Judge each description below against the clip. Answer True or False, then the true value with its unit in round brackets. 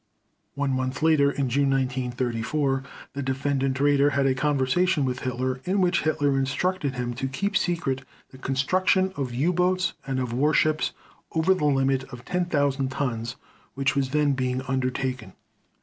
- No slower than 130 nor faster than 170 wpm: True (155 wpm)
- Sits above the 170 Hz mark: False (135 Hz)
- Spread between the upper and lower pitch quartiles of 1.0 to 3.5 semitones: True (2.5 semitones)